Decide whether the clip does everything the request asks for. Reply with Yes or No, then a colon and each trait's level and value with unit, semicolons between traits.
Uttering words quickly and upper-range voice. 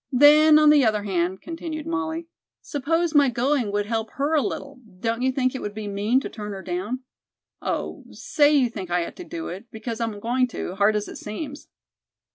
Yes: fast, 210 wpm; very high, 250 Hz